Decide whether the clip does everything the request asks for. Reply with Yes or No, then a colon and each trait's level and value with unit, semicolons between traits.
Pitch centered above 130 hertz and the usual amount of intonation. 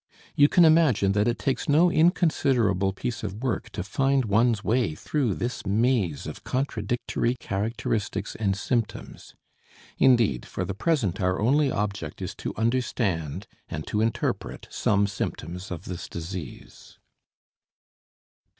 No: low, 110 Hz; average, 4.8 semitones